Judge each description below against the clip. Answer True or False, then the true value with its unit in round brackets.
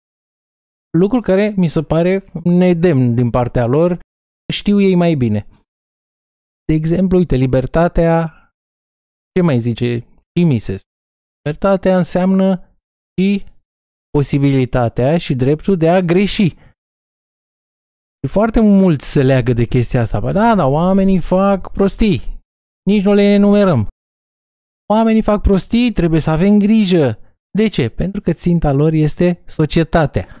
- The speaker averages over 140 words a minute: False (120 wpm)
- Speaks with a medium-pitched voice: True (165 Hz)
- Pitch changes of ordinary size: False (7.3 semitones)